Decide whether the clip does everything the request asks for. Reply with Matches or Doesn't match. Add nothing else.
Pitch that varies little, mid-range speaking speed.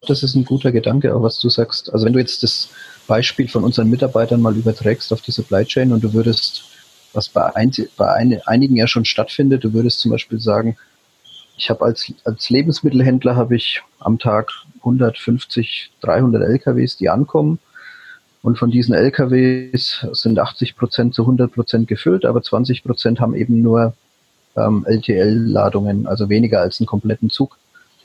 Matches